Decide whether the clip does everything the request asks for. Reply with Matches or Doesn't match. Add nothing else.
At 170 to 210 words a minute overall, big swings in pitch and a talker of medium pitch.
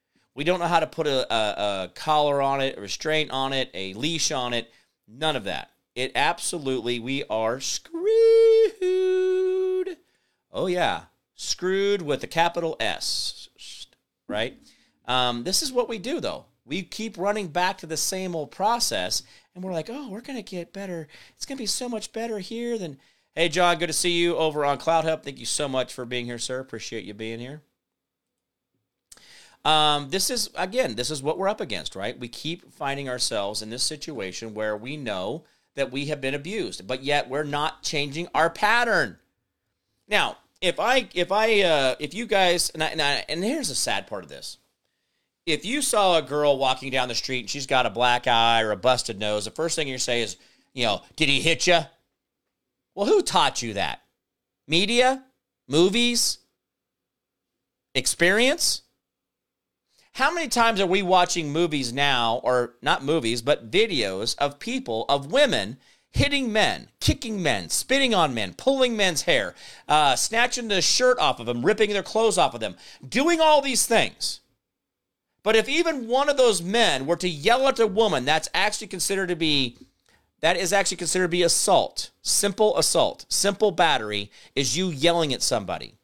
Matches